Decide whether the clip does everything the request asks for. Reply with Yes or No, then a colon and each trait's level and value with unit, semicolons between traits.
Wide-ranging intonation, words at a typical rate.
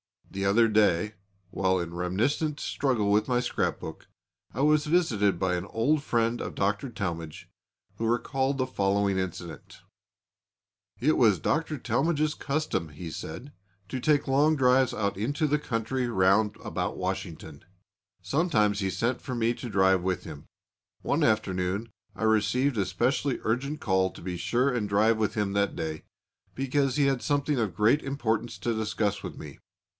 Yes: wide, 5.7 semitones; average, 160 wpm